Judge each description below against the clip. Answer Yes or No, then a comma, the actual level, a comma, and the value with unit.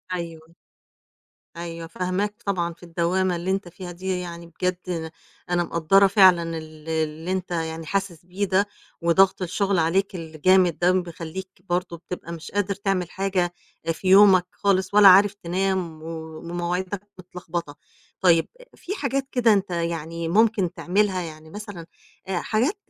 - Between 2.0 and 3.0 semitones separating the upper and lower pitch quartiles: Yes, narrow, 2.5 semitones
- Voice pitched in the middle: Yes, medium, 180 Hz